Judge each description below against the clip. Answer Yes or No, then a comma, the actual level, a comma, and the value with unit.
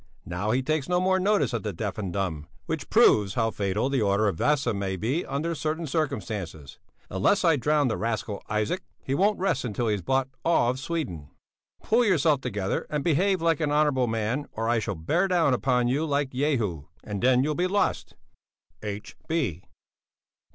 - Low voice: Yes, low, 130 Hz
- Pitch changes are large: Yes, wide, 6.8 semitones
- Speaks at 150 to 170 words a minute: No, average, 185 wpm